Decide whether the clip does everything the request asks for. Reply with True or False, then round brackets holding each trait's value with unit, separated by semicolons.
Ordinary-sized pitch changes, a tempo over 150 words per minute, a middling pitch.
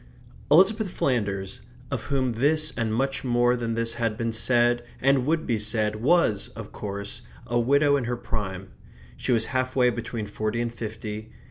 False (3.1 semitones; 170 wpm; 120 Hz)